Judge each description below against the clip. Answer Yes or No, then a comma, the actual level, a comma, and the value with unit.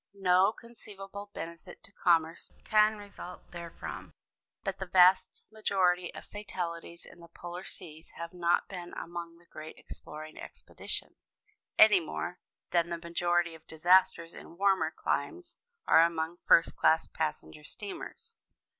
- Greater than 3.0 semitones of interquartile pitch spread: No, narrow, 2.6 semitones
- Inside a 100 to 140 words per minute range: Yes, slow, 135 wpm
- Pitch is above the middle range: No, medium, 175 Hz